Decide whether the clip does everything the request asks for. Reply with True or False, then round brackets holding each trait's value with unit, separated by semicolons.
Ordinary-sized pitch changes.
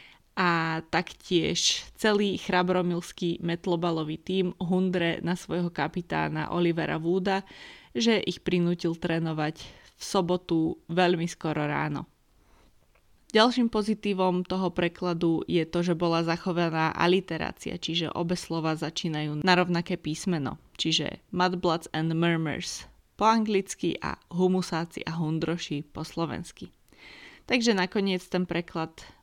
False (2.1 semitones)